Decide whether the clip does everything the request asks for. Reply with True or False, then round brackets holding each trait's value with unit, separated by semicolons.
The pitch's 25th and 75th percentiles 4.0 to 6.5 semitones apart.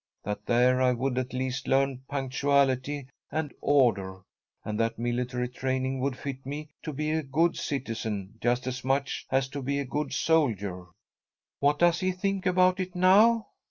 False (3.4 semitones)